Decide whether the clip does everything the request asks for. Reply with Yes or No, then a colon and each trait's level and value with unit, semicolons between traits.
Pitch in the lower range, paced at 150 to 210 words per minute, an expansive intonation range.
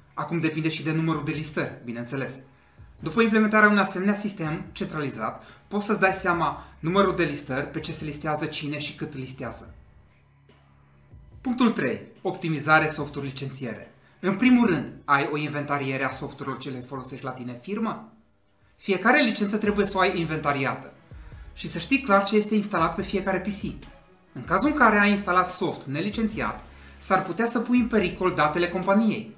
No: medium, 160 Hz; average, 165 wpm; wide, 6.5 semitones